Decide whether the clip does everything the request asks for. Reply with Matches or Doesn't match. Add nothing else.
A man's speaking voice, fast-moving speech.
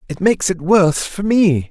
Matches